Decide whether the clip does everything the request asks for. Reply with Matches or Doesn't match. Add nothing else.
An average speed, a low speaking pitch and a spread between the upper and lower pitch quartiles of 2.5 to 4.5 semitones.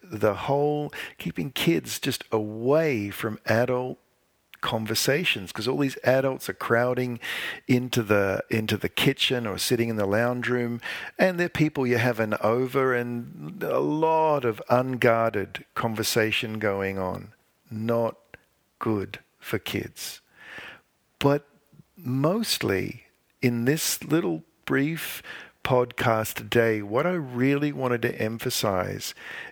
Doesn't match